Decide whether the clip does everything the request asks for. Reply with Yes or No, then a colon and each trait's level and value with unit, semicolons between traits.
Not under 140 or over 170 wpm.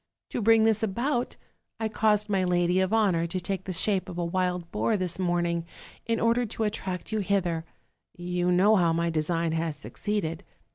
No: average, 185 wpm